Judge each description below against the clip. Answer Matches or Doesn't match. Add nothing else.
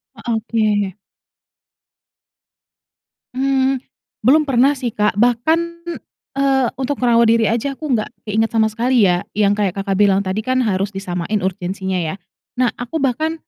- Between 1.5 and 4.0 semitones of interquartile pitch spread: Doesn't match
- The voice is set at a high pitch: Matches